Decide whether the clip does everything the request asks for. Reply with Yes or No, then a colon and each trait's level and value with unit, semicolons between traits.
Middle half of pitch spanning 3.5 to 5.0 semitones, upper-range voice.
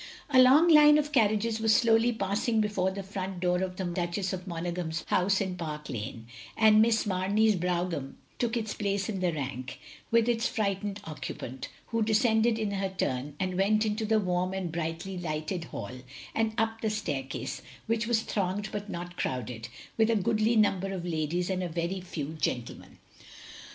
Yes: average, 4.1 semitones; high, 195 Hz